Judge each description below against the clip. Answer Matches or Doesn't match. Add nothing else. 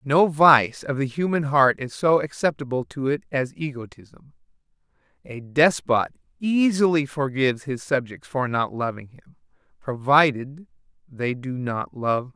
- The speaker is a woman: Doesn't match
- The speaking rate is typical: Matches